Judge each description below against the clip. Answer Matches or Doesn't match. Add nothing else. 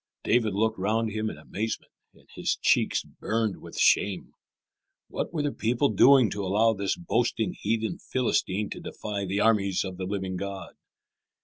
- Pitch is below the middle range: Matches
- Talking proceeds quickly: Doesn't match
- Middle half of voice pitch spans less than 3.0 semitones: Matches